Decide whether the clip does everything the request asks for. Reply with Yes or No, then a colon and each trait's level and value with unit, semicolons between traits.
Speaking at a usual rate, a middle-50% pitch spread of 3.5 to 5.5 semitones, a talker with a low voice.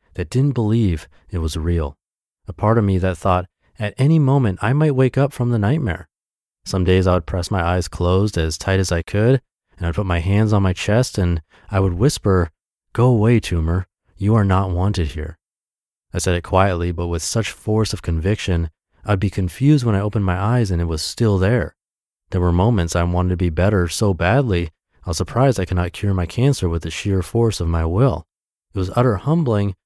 No: fast, 215 wpm; average, 4.1 semitones; very low, 95 Hz